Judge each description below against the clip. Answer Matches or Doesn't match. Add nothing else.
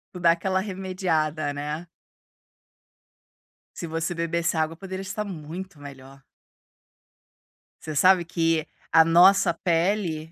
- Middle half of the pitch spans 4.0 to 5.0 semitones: Doesn't match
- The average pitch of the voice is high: Doesn't match